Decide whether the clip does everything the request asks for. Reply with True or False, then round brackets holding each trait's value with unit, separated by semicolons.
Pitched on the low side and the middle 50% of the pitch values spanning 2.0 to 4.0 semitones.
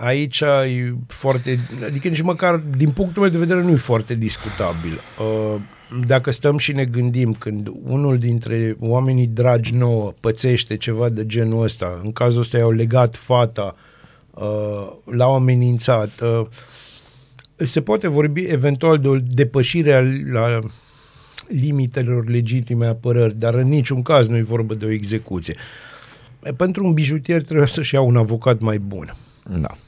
True (125 Hz; 3.6 semitones)